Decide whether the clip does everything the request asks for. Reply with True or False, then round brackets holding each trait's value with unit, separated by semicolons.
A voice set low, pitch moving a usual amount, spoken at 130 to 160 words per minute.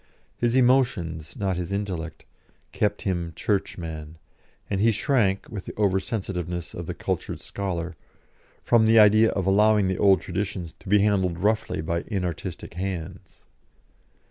True (95 Hz; 3.2 semitones; 145 wpm)